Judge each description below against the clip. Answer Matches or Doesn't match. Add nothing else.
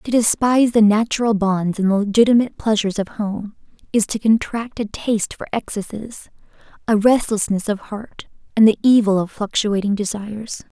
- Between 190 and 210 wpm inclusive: Doesn't match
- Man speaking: Doesn't match